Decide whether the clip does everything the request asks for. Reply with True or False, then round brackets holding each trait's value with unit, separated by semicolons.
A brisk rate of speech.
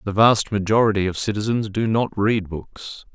False (170 wpm)